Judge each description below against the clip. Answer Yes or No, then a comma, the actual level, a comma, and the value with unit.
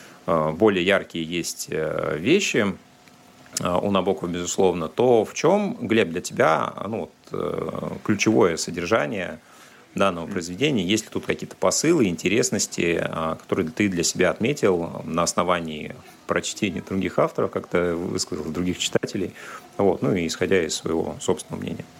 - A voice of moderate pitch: No, very low, 90 Hz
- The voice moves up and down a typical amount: No, narrow, 1.9 semitones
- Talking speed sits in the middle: Yes, average, 130 wpm